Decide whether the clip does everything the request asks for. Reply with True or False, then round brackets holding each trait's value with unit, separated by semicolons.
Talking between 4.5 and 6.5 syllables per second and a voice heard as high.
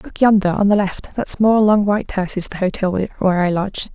True (6.1 syllables/s; 200 Hz)